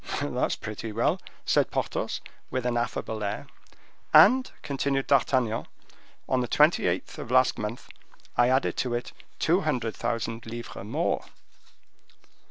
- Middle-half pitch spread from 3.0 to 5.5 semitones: No, narrow, 2.5 semitones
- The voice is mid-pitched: No, low, 120 Hz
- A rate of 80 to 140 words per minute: Yes, slow, 135 wpm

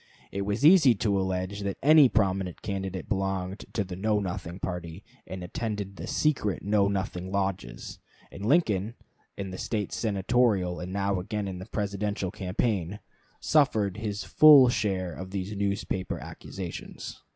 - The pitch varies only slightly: Yes, narrow, 2.2 semitones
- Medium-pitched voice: No, low, 100 Hz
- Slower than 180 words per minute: Yes, average, 150 wpm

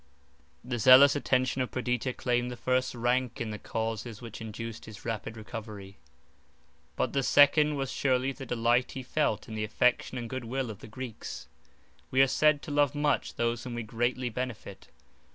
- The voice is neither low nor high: No, low, 125 Hz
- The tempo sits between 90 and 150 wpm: No, average, 180 wpm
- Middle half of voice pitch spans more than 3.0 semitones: No, narrow, 2.4 semitones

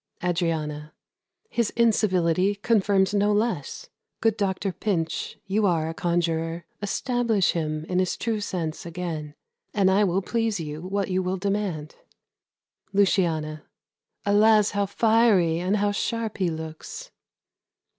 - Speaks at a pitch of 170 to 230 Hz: Yes, high, 190 Hz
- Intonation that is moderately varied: Yes, average, 3.9 semitones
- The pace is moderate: No, slow, 125 wpm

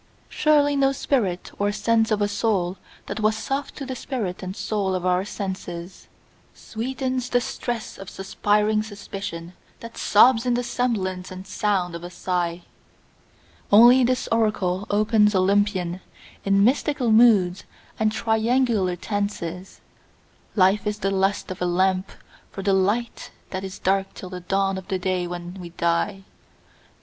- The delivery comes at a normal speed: Yes, average, 150 wpm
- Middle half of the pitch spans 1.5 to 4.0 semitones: Yes, average, 3.4 semitones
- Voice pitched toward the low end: No, high, 200 Hz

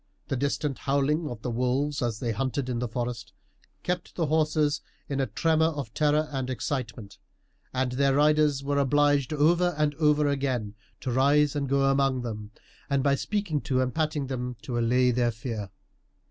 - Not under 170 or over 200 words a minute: Yes, average, 175 wpm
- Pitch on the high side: No, medium, 140 Hz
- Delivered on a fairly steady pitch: No, average, 3.1 semitones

